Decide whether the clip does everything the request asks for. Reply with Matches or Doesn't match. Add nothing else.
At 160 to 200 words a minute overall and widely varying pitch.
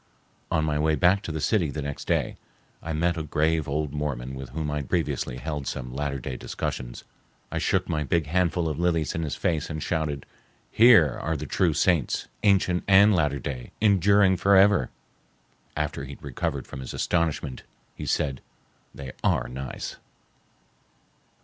Doesn't match